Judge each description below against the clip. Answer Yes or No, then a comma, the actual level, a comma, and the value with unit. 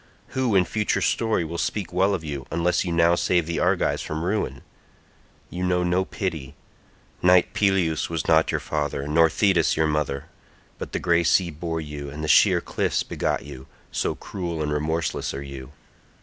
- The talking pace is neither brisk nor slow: Yes, average, 180 wpm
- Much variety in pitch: No, average, 3.2 semitones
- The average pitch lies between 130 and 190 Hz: No, very low, 85 Hz